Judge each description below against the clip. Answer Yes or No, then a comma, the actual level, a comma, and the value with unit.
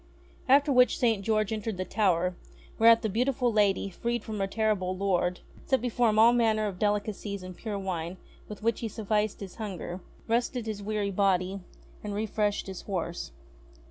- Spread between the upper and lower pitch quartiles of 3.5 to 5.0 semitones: No, narrow, 2.6 semitones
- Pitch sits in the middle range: No, high, 210 Hz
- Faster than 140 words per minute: Yes, average, 175 wpm